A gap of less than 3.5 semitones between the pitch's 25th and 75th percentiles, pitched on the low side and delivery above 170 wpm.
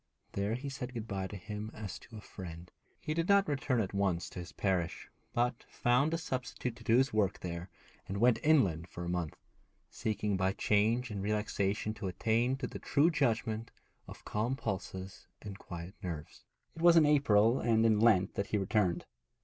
No: average, 4.5 semitones; low, 105 Hz; average, 190 wpm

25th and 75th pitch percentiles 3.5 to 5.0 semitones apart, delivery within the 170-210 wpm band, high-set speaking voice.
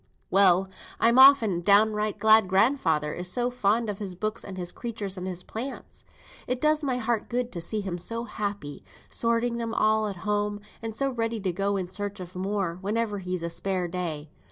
Yes: average, 3.8 semitones; average, 195 wpm; high, 205 Hz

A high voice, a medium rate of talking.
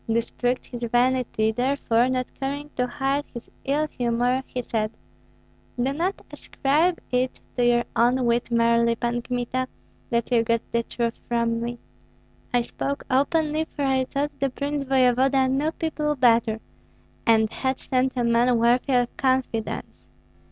Yes: very high, 250 Hz; average, 150 wpm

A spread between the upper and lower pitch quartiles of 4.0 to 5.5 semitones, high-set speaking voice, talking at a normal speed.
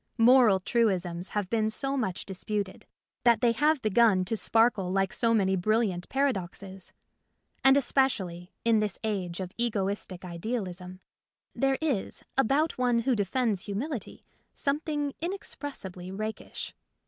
No: average, 5.0 semitones; high, 215 Hz; slow, 125 wpm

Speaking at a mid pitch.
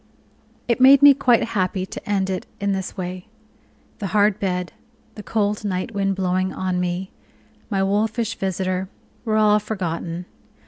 No: high, 195 Hz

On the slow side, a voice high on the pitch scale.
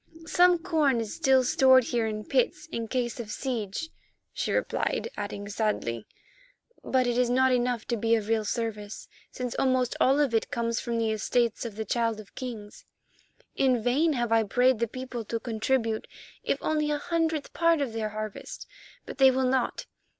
No: average, 180 wpm; high, 240 Hz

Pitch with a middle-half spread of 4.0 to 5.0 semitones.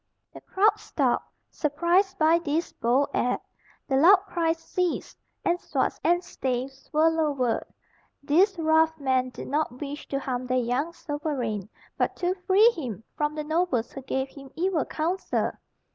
Yes: average, 4.5 semitones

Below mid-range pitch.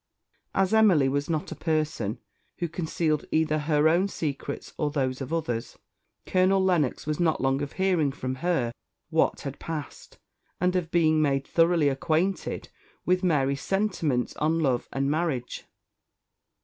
No: medium, 155 Hz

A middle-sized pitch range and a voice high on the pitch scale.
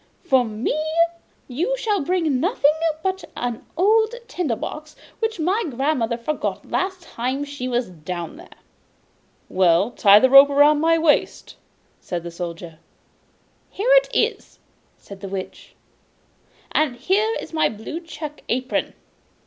No: wide, 7.5 semitones; very high, 285 Hz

